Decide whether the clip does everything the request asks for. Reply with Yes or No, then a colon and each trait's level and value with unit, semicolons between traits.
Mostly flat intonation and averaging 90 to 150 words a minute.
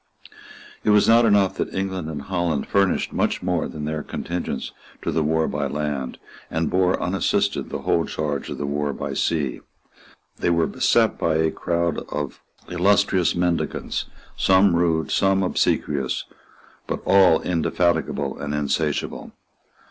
No: average, 3.8 semitones; average, 145 wpm